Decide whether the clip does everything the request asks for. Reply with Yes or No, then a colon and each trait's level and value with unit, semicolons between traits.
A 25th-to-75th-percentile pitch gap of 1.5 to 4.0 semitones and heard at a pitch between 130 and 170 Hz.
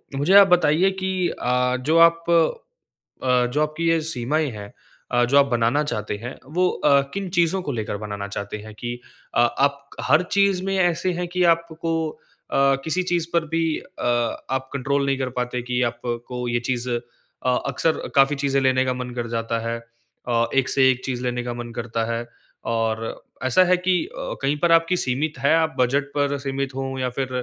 No: average, 5.0 semitones; low, 135 Hz